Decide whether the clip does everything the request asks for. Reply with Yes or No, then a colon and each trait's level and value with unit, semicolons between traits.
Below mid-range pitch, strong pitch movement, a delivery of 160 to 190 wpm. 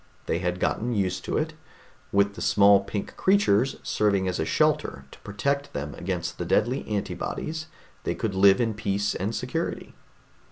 No: low, 100 Hz; average, 3.5 semitones; average, 165 wpm